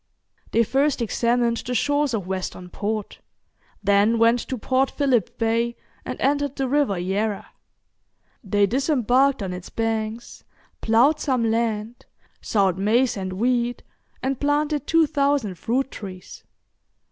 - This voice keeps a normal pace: No, slow, 130 wpm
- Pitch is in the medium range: No, high, 235 Hz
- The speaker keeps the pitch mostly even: No, average, 4.4 semitones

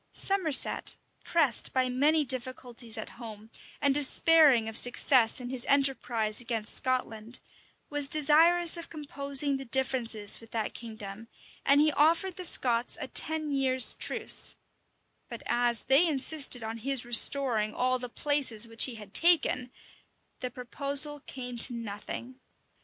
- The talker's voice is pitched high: Yes, very high, 255 Hz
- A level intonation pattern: No, average, 3.8 semitones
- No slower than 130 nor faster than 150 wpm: Yes, average, 140 wpm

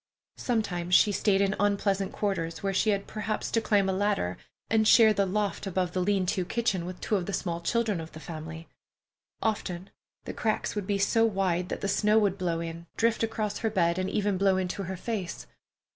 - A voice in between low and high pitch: No, high, 195 Hz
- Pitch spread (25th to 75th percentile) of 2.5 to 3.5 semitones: Yes, average, 2.9 semitones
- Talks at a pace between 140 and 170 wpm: No, fast, 205 wpm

